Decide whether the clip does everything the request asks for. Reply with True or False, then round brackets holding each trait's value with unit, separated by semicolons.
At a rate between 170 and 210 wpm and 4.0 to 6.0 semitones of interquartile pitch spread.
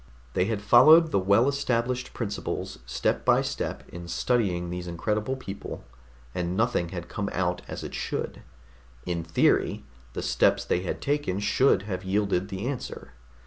False (155 wpm; 5.3 semitones)